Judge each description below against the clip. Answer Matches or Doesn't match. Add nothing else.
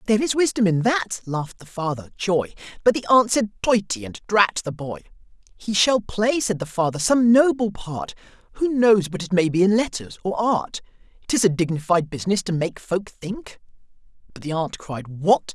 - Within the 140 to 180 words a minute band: Doesn't match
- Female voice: Doesn't match